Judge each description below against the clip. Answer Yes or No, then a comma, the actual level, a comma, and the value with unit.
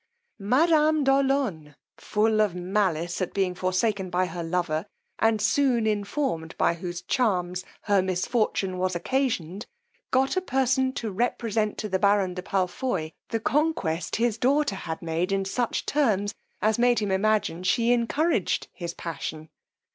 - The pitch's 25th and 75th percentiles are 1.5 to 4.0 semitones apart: No, average, 5.2 semitones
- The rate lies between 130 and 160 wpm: Yes, average, 145 wpm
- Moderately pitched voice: No, high, 205 Hz